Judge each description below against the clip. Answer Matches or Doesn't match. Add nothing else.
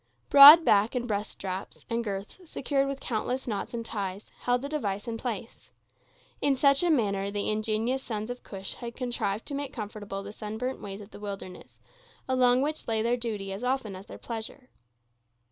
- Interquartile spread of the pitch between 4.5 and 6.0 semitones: Doesn't match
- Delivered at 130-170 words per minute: Doesn't match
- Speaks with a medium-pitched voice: Doesn't match